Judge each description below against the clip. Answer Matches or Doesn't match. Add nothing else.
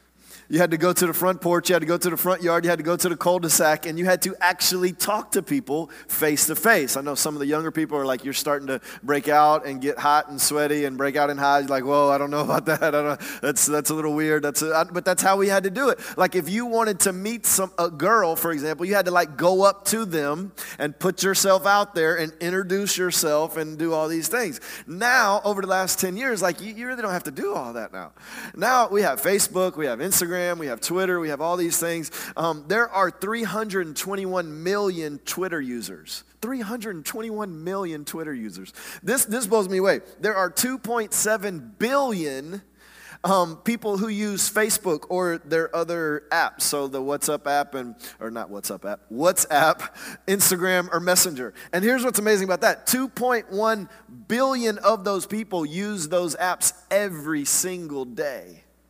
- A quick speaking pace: Matches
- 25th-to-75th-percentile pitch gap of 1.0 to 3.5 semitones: Doesn't match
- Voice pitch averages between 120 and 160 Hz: Doesn't match